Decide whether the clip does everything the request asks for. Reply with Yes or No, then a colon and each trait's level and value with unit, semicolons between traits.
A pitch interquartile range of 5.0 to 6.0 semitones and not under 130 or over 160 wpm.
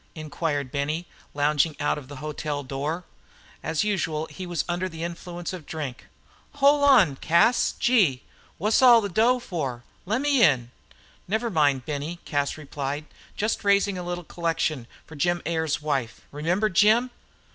Yes: wide, 5.4 semitones; average, 150 wpm